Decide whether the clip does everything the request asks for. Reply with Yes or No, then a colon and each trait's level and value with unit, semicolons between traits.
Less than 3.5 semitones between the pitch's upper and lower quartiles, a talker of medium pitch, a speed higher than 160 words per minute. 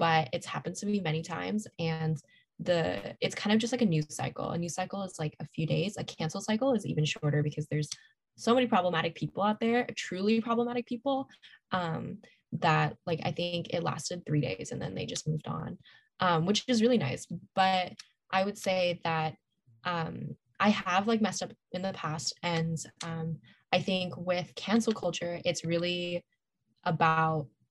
No: average, 4.2 semitones; medium, 175 Hz; average, 185 wpm